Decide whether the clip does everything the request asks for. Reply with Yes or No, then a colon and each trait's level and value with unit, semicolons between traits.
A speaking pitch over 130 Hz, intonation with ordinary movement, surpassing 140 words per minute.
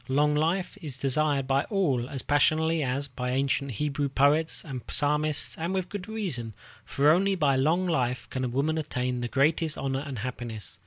Yes: medium, 140 Hz; average, 3.5 semitones; average, 180 wpm